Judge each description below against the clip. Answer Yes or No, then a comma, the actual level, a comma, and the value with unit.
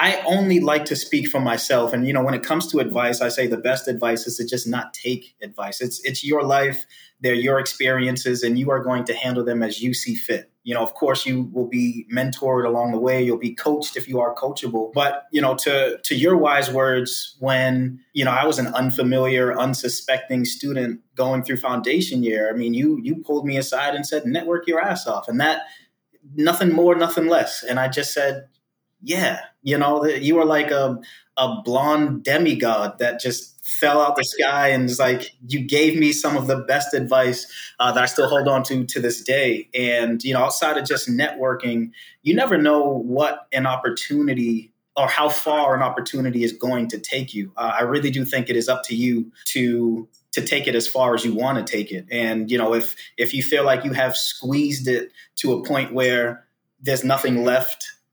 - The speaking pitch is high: No, low, 130 Hz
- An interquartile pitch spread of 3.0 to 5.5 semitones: No, narrow, 2.6 semitones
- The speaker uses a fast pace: Yes, fast, 215 wpm